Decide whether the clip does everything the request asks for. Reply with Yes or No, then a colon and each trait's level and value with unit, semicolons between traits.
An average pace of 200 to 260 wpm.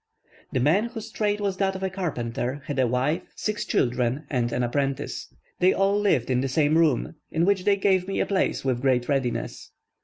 Yes: fast, 205 wpm